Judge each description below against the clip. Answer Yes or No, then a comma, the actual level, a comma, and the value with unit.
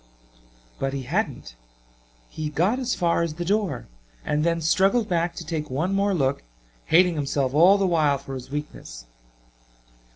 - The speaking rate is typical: Yes, average, 160 wpm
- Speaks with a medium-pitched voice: Yes, medium, 165 Hz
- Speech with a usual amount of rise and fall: Yes, average, 4.8 semitones